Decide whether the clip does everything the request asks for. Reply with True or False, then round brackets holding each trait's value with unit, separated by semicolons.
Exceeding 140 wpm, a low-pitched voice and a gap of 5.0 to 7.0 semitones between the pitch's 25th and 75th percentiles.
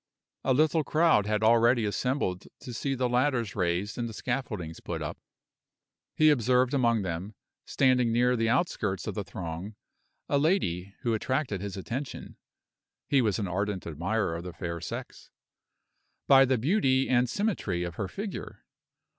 True (155 wpm; 115 Hz; 5.3 semitones)